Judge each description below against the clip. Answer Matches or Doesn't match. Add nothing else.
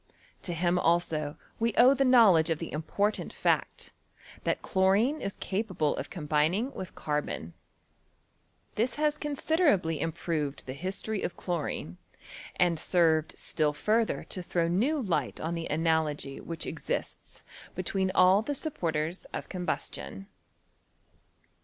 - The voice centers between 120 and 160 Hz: Doesn't match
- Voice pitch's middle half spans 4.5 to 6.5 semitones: Matches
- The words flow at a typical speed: Doesn't match